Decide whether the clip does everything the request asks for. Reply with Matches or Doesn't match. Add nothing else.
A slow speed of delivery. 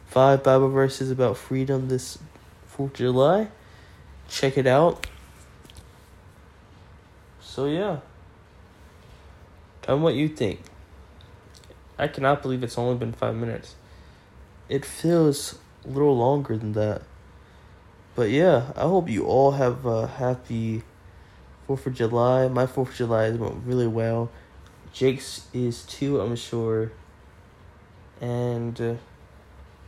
Matches